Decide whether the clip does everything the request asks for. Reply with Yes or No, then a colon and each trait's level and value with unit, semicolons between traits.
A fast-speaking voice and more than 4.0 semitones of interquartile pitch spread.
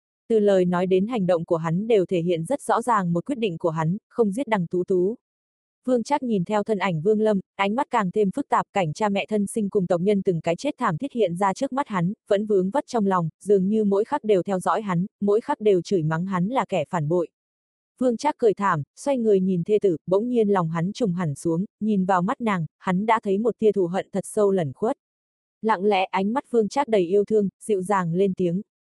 No: fast, 255 wpm; average, 3.1 semitones